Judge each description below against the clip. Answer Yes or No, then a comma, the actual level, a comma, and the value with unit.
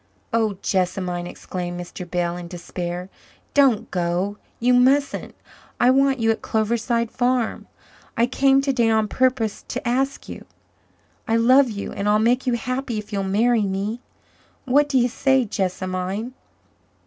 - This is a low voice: No, high, 225 Hz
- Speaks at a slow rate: No, average, 150 wpm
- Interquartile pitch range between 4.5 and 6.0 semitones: Yes, average, 4.8 semitones